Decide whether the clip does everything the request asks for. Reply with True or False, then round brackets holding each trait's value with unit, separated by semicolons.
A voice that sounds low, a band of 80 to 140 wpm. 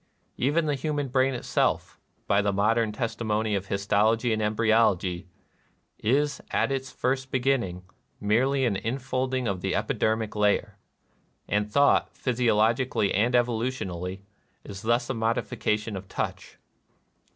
True (115 Hz; 135 wpm)